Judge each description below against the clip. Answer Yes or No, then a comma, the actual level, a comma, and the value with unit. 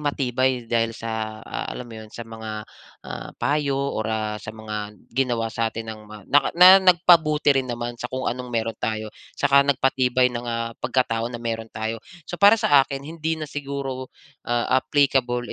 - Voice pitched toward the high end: No, low, 120 Hz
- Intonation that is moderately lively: Yes, average, 3.7 semitones